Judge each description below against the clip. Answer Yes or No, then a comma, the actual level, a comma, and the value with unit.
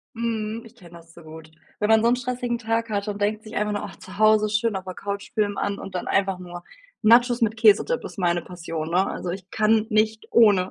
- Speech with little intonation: No, average, 3.3 semitones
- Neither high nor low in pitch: No, high, 210 Hz